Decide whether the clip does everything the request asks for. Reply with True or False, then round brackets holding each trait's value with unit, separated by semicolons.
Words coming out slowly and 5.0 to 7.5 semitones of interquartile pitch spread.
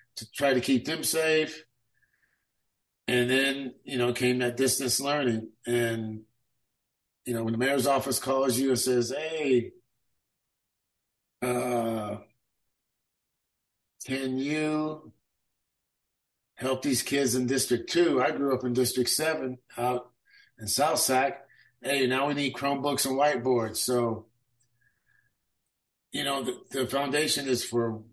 False (130 wpm; 2.5 semitones)